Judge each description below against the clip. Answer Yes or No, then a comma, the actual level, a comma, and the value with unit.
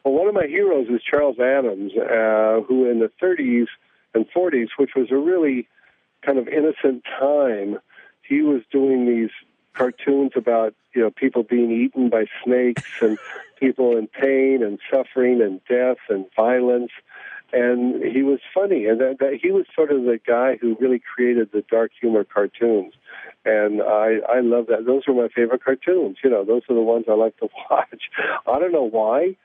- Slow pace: No, average, 185 wpm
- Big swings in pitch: No, average, 2.8 semitones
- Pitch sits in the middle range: No, low, 125 Hz